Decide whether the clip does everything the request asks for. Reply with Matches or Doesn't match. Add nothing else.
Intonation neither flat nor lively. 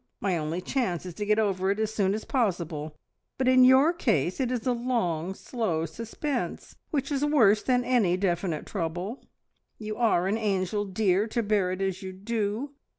Matches